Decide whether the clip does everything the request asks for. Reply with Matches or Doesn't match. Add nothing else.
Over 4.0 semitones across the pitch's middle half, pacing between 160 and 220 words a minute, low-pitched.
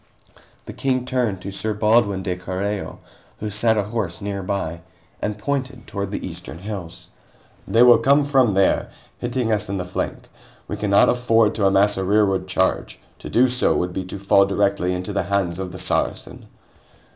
Doesn't match